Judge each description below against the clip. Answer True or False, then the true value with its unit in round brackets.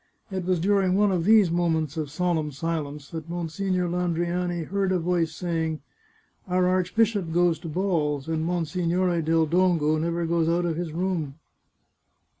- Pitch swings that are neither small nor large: False (2.1 semitones)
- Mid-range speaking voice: True (170 Hz)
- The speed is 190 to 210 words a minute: False (165 wpm)